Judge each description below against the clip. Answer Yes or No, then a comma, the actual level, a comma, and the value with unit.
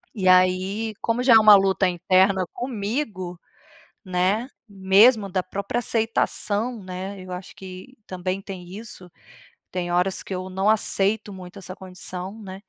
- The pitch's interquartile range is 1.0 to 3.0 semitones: Yes, narrow, 2.5 semitones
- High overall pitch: Yes, high, 195 Hz